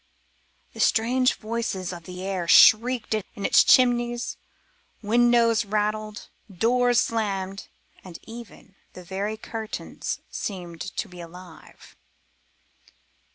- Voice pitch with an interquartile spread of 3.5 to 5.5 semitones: Yes, average, 3.8 semitones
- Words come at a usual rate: No, slow, 110 wpm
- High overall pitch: Yes, high, 215 Hz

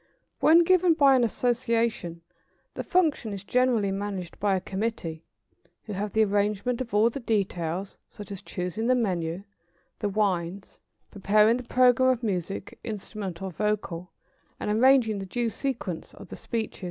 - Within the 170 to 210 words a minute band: No, average, 160 wpm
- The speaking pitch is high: Yes, high, 210 Hz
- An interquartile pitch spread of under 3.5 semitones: No, average, 3.9 semitones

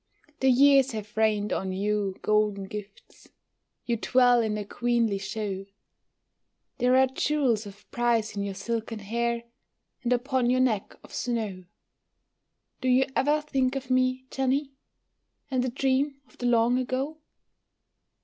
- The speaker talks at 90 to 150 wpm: Yes, average, 140 wpm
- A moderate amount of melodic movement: Yes, average, 3.6 semitones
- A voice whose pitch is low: No, high, 240 Hz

